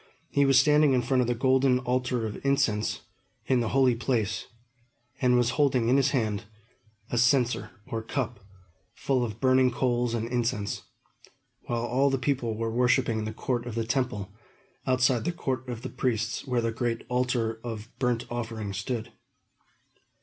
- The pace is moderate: Yes, average, 170 wpm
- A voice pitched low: Yes, low, 120 Hz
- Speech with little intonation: Yes, narrow, 2.3 semitones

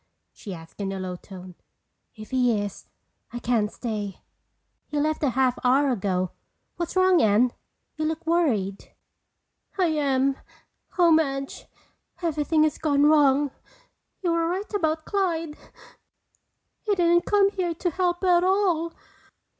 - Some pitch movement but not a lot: No, wide, 6.2 semitones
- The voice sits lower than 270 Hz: No, very high, 300 Hz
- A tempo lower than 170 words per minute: Yes, average, 140 wpm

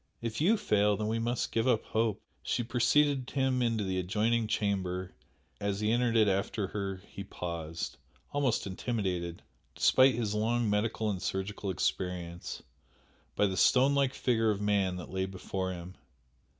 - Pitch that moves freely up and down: No, average, 3.7 semitones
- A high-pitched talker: No, low, 105 Hz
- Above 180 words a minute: No, average, 160 wpm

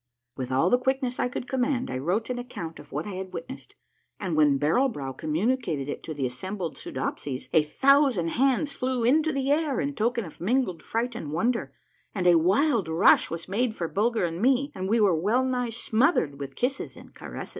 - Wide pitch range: Yes, wide, 7.6 semitones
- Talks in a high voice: Yes, high, 220 Hz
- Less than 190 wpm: No, fast, 205 wpm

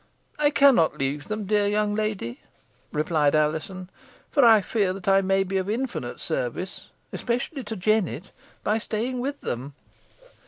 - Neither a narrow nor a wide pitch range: Yes, average, 4.1 semitones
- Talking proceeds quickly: No, average, 145 wpm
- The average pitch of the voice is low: No, high, 205 Hz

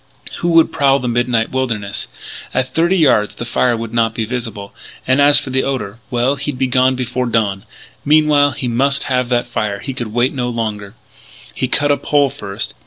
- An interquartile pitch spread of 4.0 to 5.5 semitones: No, average, 3.1 semitones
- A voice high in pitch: No, low, 125 Hz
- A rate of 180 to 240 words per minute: Yes, average, 195 wpm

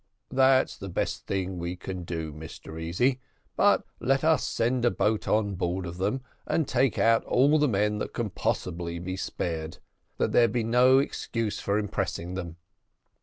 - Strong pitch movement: Yes, wide, 5.9 semitones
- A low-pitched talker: Yes, low, 105 Hz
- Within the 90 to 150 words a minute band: No, average, 175 wpm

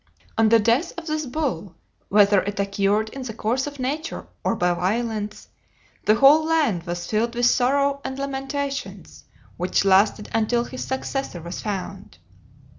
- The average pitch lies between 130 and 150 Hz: No, high, 230 Hz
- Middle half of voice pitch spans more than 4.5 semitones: Yes, average, 5.3 semitones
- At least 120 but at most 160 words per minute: Yes, average, 155 wpm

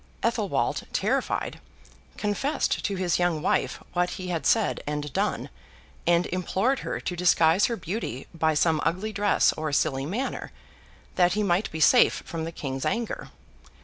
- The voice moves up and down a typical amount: Yes, average, 4.3 semitones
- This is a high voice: No, medium, 175 Hz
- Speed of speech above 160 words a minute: No, average, 155 wpm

